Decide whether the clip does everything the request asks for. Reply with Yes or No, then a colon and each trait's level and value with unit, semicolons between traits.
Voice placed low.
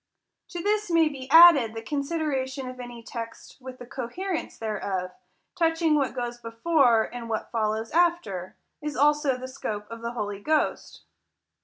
No: very high, 260 Hz